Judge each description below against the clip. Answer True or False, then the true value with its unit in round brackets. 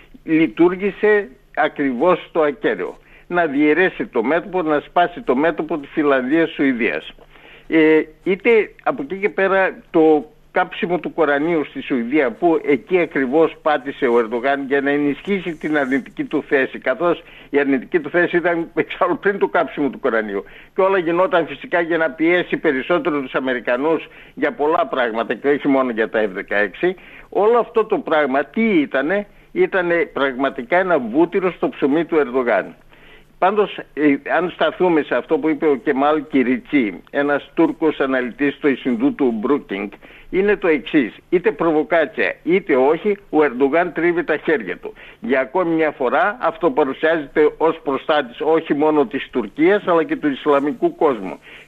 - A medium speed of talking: True (155 wpm)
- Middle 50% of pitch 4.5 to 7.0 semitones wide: True (4.9 semitones)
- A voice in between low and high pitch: True (165 Hz)